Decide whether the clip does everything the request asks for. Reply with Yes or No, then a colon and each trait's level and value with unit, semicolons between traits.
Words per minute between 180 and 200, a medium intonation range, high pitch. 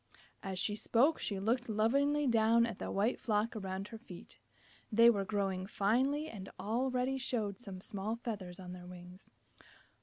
No: average, 160 wpm; average, 3.8 semitones; high, 215 Hz